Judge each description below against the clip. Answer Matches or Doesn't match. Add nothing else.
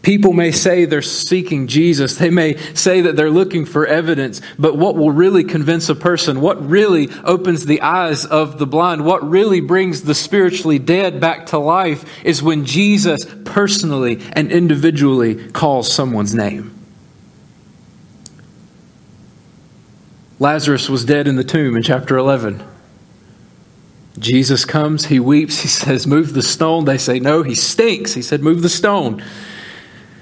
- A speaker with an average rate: Matches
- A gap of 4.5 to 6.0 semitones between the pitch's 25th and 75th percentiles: Doesn't match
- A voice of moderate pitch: Matches